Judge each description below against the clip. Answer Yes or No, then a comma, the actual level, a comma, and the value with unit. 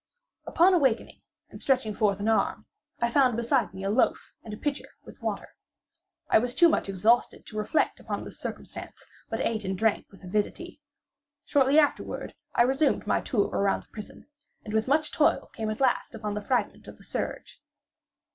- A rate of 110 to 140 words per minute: No, average, 185 wpm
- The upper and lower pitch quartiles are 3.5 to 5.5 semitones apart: Yes, average, 4.3 semitones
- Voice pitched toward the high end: Yes, high, 230 Hz